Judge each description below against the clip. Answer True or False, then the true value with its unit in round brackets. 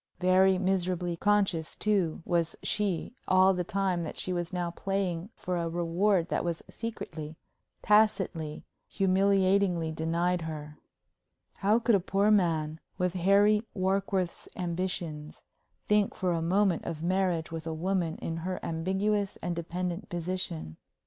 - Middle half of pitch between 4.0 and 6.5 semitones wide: False (2.6 semitones)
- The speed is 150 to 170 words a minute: False (135 wpm)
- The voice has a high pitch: False (180 Hz)